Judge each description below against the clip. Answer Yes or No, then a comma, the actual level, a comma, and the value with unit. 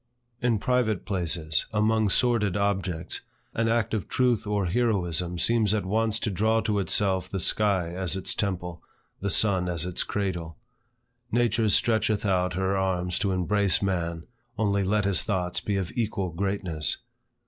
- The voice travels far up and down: No, average, 3.1 semitones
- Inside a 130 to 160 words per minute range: Yes, average, 155 wpm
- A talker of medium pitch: No, low, 100 Hz